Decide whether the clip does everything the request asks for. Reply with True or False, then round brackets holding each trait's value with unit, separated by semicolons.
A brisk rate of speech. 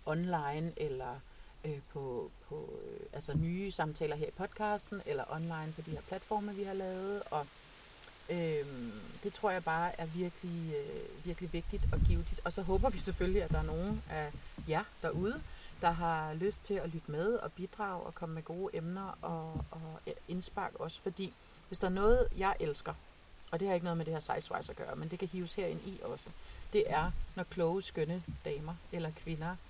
False (200 wpm)